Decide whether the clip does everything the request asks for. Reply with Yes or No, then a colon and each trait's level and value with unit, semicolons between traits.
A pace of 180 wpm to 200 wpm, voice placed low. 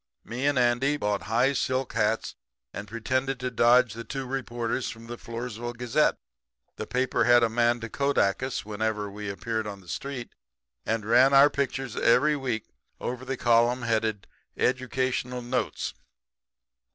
No: average, 155 wpm; low, 120 Hz